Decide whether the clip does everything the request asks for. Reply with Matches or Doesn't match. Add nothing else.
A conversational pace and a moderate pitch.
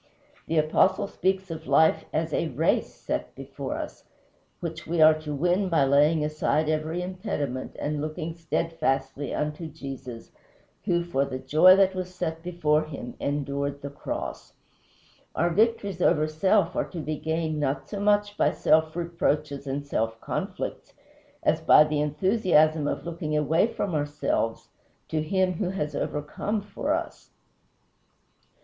Matches